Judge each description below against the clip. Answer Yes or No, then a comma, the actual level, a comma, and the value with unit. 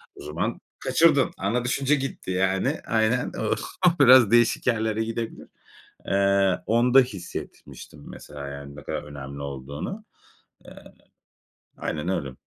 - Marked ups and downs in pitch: Yes, wide, 8.9 semitones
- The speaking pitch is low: Yes, low, 100 Hz